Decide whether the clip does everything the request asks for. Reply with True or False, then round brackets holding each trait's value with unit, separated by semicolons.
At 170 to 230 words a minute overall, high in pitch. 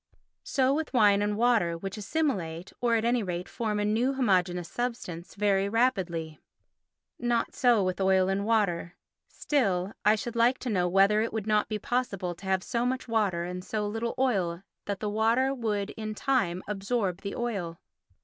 True (180 wpm; 210 Hz)